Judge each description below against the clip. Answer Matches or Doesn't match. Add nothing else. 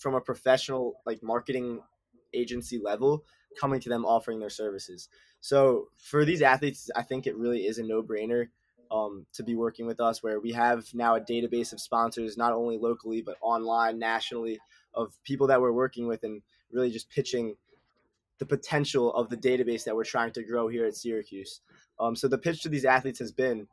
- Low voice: Matches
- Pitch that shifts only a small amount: Matches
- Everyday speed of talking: Matches